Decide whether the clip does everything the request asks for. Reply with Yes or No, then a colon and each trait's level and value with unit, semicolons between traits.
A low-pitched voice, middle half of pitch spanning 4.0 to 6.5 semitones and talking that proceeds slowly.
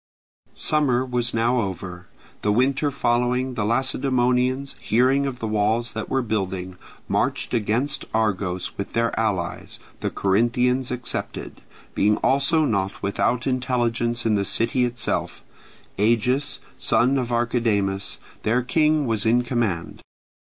No: low, 120 Hz; average, 3.2 semitones; slow, 125 wpm